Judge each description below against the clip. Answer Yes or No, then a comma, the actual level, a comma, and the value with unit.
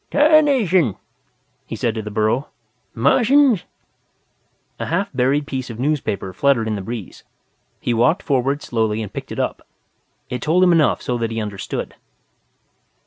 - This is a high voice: No, low, 130 Hz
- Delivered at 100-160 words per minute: Yes, average, 150 wpm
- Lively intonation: Yes, wide, 7.1 semitones